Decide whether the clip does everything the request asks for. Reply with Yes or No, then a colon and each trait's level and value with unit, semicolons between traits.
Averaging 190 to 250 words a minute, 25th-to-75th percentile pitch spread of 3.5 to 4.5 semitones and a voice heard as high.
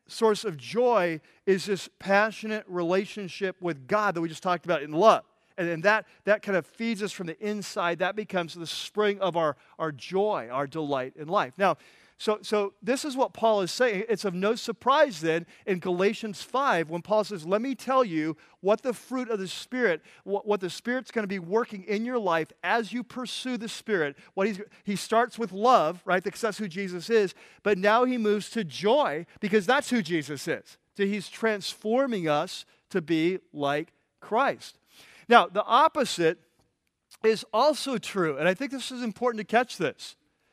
Yes: average, 195 wpm; average, 4.2 semitones; high, 205 Hz